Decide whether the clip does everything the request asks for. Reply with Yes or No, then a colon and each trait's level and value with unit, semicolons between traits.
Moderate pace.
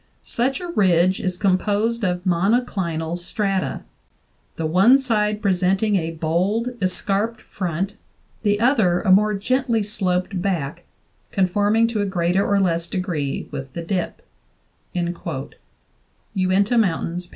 No: slow, 125 wpm